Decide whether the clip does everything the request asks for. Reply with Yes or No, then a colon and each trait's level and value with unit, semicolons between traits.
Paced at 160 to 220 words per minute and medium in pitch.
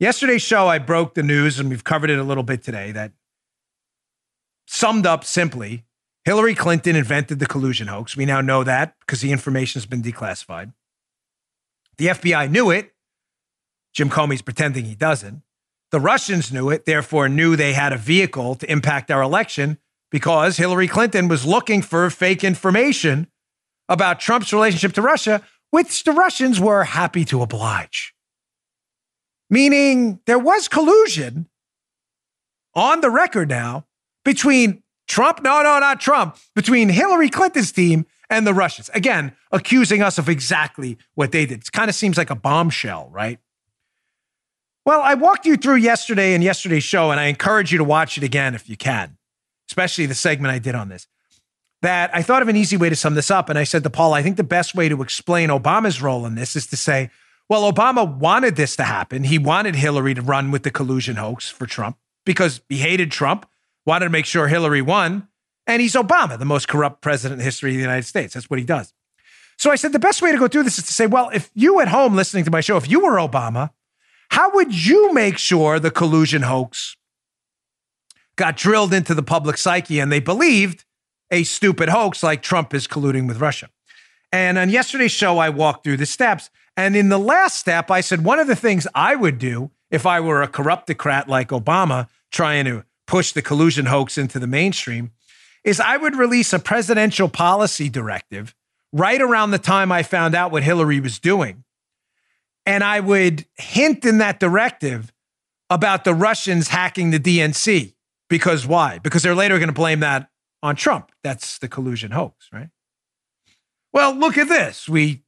Yes: average, 185 wpm; medium, 165 Hz